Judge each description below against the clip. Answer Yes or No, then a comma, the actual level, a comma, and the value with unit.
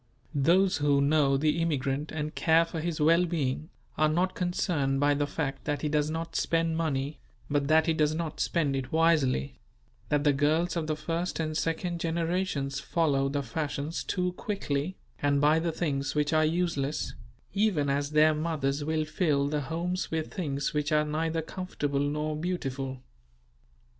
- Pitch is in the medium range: Yes, medium, 155 Hz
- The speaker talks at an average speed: Yes, average, 170 wpm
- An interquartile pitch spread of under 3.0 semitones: Yes, narrow, 2.6 semitones